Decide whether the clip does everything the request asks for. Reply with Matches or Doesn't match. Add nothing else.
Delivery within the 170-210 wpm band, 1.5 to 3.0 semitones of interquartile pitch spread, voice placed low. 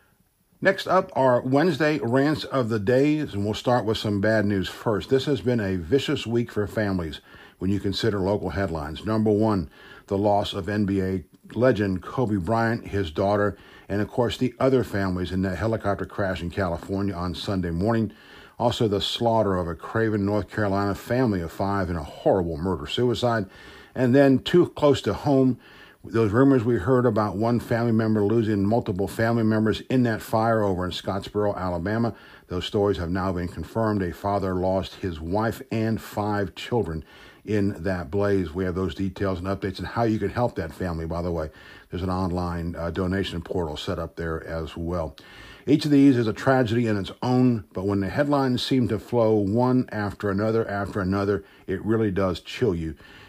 Doesn't match